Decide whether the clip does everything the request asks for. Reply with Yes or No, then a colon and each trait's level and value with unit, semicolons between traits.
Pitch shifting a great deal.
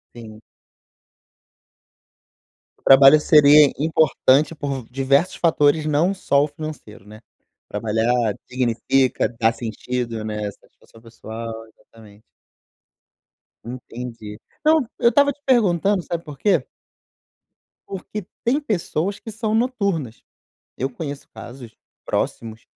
Yes: wide, 6.8 semitones